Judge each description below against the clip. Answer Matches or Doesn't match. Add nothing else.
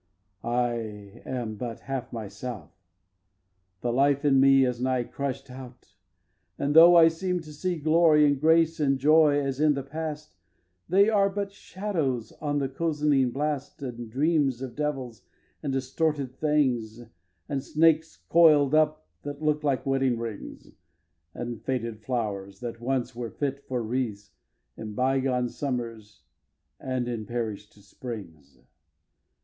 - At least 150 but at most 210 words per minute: Doesn't match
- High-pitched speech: Doesn't match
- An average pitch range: Matches